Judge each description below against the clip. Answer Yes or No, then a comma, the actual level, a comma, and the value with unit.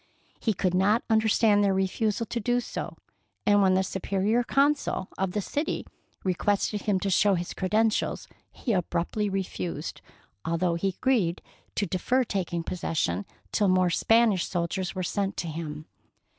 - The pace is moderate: Yes, average, 155 wpm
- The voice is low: No, high, 195 Hz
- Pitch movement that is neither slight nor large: Yes, average, 3.2 semitones